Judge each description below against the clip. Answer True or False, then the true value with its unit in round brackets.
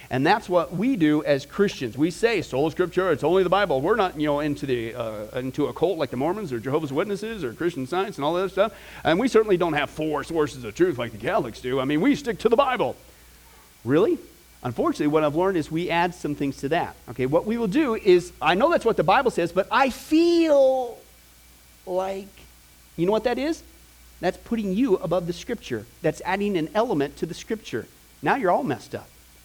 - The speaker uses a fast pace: True (225 wpm)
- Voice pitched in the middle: True (175 Hz)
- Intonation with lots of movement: True (7.1 semitones)